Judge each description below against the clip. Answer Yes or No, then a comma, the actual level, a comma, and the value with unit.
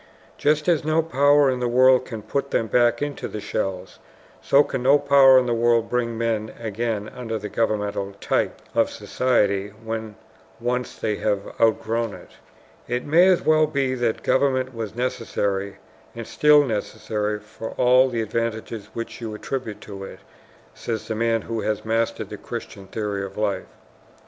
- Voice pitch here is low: Yes, low, 115 Hz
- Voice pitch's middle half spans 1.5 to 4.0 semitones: Yes, average, 3.3 semitones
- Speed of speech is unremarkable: Yes, average, 170 wpm